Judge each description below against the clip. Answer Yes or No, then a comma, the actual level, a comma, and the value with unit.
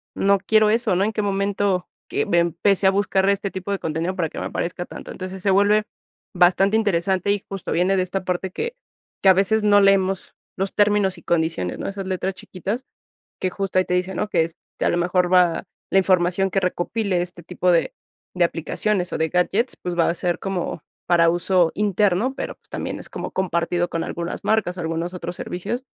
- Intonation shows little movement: Yes, narrow, 2.2 semitones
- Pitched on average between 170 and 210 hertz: Yes, medium, 185 Hz